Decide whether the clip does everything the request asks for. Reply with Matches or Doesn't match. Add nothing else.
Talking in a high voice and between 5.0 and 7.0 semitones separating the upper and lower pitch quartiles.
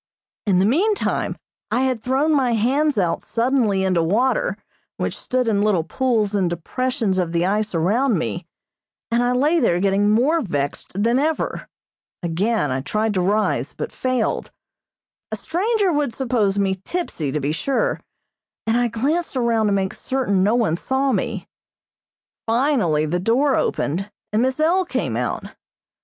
Matches